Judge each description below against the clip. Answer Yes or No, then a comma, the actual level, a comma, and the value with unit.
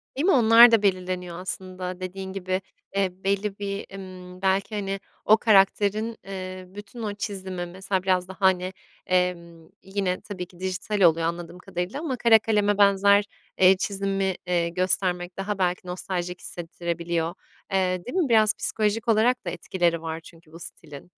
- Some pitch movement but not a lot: No, narrow, 2.2 semitones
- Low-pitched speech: No, high, 190 Hz